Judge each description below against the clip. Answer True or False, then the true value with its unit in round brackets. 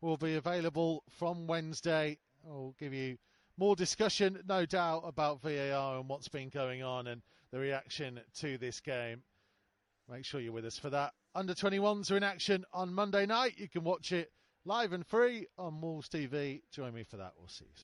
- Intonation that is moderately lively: False (5.8 semitones)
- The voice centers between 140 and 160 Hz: True (150 Hz)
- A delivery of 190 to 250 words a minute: True (195 wpm)